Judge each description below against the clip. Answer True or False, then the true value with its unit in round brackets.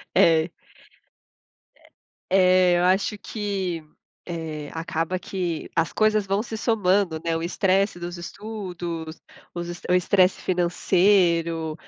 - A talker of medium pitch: True (175 Hz)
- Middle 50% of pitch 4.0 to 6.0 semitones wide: False (2.9 semitones)